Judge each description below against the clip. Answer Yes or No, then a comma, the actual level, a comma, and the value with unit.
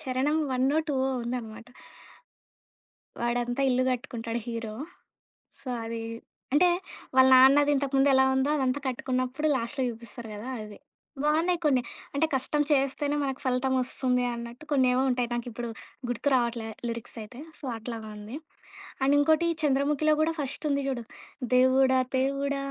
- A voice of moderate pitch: No, very high, 260 Hz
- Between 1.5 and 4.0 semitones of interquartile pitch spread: Yes, average, 2.8 semitones